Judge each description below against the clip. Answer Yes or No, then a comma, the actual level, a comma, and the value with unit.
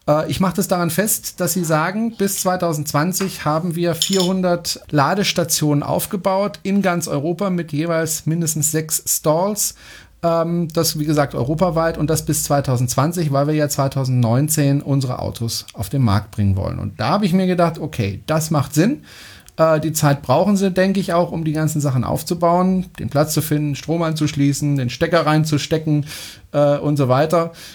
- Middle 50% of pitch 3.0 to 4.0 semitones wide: Yes, average, 3.3 semitones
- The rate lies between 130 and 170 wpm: Yes, average, 165 wpm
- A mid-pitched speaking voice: Yes, medium, 155 Hz